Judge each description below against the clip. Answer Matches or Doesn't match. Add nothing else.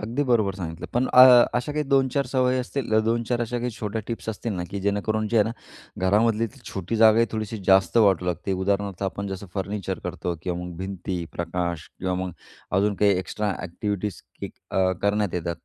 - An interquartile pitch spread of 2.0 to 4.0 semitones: Matches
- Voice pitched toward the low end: Matches